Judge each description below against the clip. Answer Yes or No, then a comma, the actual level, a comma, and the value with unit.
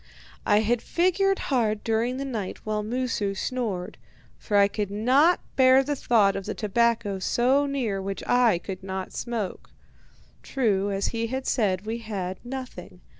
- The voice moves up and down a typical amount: Yes, average, 4.3 semitones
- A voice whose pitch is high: Yes, high, 225 Hz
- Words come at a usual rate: Yes, average, 155 wpm